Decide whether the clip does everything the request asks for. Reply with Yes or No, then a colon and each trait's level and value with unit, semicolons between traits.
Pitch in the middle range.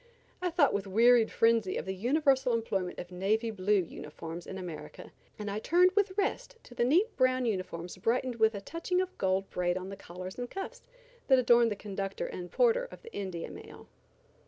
No: high, 220 Hz